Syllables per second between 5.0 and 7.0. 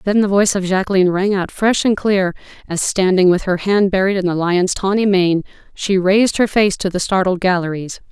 Yes: 5.5 syllables/s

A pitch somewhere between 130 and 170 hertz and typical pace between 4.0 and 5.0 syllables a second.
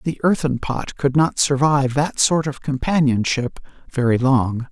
Yes: low, 135 Hz; 4.4 syllables/s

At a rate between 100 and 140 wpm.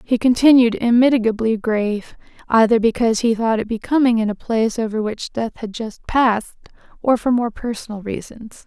No: average, 165 wpm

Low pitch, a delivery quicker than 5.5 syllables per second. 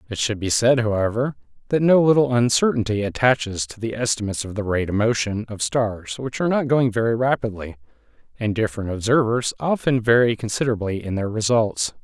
Yes: low, 115 Hz; 5.8 syllables/s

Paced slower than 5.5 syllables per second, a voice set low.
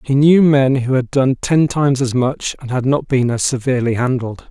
Yes: 5.0 syllables/s; low, 130 Hz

